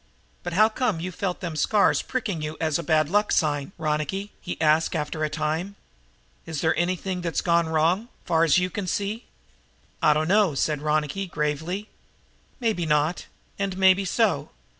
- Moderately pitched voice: Yes, medium, 170 Hz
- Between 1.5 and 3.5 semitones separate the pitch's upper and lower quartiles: No, average, 4.0 semitones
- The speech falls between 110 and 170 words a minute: Yes, average, 160 wpm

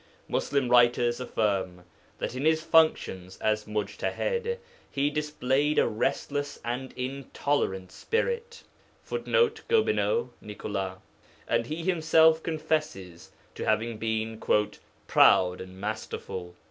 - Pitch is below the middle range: Yes, low, 125 Hz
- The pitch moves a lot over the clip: Yes, wide, 6.9 semitones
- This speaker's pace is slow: Yes, slow, 105 wpm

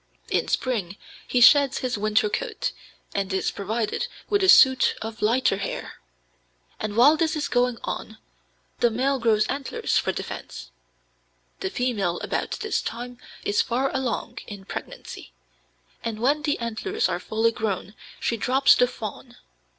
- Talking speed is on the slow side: No, average, 150 wpm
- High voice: Yes, high, 240 Hz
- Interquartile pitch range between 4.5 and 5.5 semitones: No, average, 3.8 semitones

